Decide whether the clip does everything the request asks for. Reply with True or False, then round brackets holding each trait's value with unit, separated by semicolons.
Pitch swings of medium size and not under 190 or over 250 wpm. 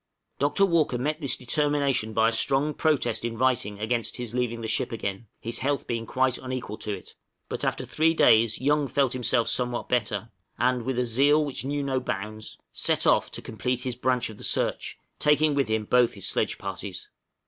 True (3.5 semitones; 195 wpm)